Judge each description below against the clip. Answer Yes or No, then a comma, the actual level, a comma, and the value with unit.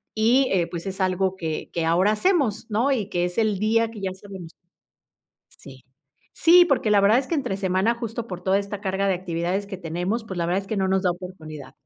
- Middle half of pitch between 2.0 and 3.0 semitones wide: No, average, 3.5 semitones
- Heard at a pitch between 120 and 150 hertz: No, high, 195 Hz